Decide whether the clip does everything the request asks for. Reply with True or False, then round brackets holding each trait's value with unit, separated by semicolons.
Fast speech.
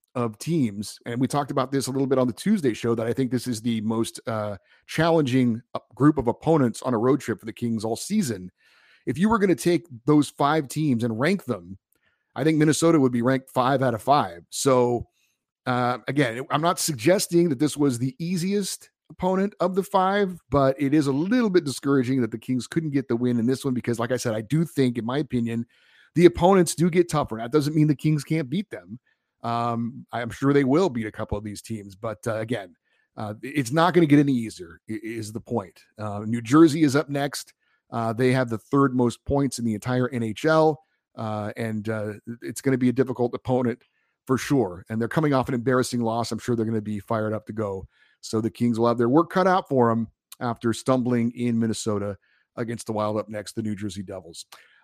True (225 wpm)